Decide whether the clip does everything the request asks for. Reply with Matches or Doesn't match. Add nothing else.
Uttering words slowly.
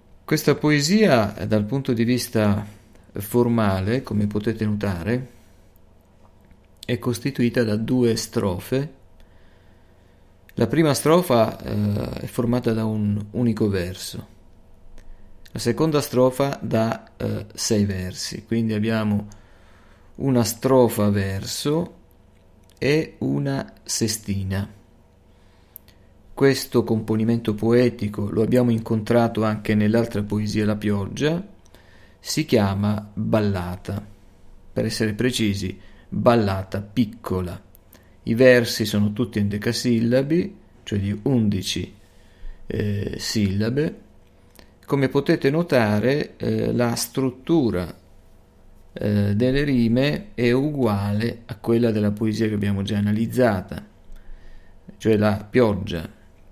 Matches